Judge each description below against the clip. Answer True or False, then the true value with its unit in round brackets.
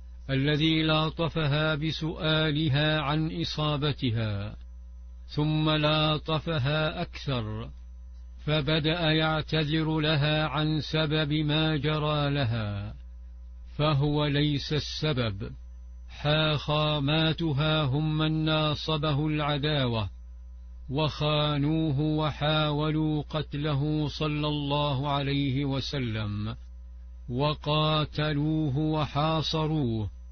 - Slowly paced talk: True (65 wpm)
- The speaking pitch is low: False (150 Hz)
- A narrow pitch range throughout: False (3.4 semitones)